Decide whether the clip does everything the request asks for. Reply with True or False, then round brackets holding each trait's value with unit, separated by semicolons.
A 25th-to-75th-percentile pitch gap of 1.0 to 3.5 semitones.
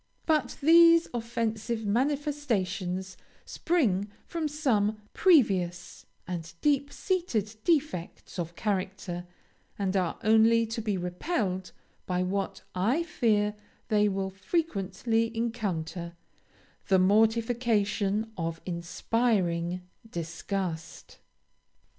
False (4.6 semitones)